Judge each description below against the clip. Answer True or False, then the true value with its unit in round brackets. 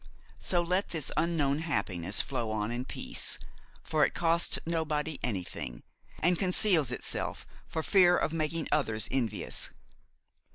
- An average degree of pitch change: False (5.7 semitones)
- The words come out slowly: True (130 wpm)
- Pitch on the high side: False (155 Hz)